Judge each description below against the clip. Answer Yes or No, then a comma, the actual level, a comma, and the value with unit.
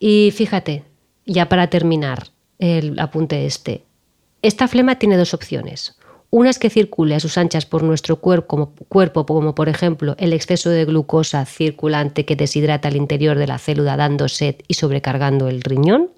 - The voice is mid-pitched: Yes, medium, 155 Hz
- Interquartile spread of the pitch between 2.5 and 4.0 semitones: Yes, average, 3.3 semitones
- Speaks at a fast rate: No, average, 165 wpm